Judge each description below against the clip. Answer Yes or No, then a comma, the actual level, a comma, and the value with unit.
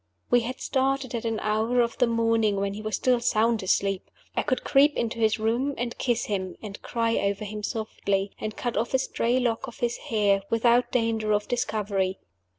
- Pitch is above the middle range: Yes, high, 230 Hz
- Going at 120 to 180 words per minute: No, average, 200 wpm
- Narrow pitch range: Yes, narrow, 2.3 semitones